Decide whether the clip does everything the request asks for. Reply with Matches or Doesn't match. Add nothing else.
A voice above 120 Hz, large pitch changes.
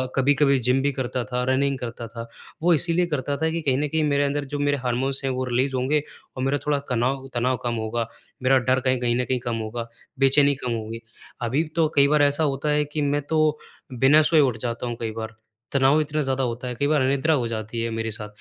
Doesn't match